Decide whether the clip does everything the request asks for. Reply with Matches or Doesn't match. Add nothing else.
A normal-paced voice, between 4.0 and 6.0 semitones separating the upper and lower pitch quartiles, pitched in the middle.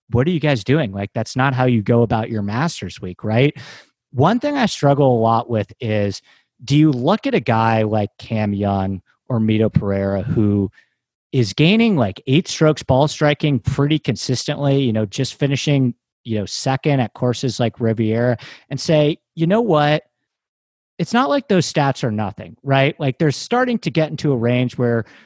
Doesn't match